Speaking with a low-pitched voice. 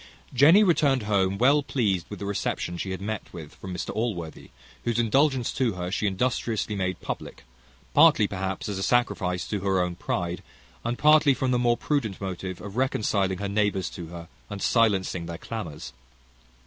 Yes: low, 100 Hz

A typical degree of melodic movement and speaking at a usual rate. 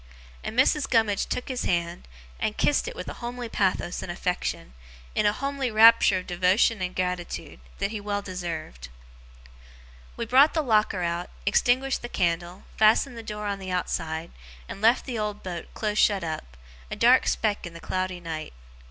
Yes: average, 4.6 semitones; average, 180 wpm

